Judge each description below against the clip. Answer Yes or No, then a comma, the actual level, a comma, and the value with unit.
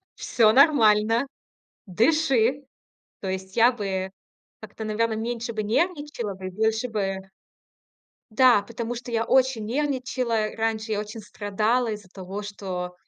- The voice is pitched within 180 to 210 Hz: No, high, 220 Hz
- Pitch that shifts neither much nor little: Yes, average, 3.0 semitones